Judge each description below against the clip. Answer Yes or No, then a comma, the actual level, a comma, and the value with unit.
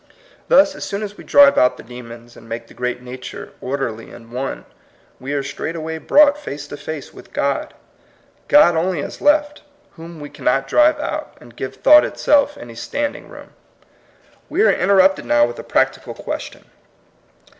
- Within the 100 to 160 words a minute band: No, average, 175 wpm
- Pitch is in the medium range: Yes, medium, 150 Hz